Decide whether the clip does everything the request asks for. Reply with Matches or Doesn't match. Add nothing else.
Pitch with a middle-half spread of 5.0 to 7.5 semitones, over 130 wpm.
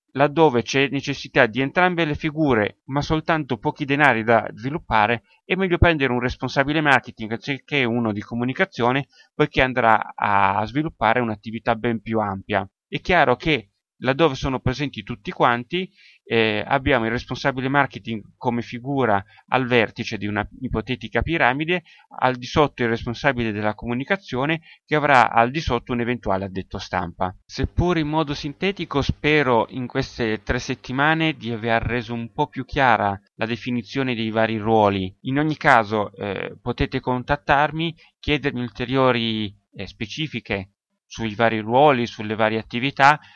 Doesn't match